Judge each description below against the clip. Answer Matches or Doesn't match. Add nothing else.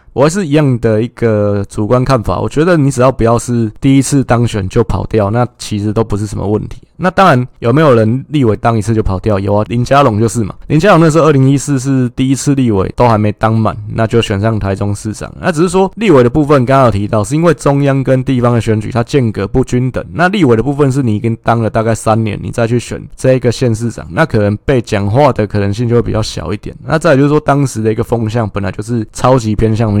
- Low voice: Matches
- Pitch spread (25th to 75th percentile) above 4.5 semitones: Doesn't match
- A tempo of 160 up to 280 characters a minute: Doesn't match